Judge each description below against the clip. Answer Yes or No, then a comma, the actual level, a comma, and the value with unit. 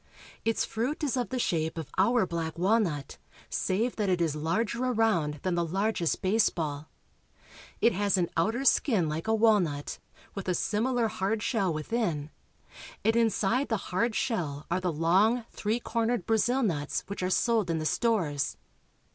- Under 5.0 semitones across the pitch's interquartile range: No, wide, 5.4 semitones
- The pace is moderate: Yes, average, 165 wpm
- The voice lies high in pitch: Yes, high, 195 Hz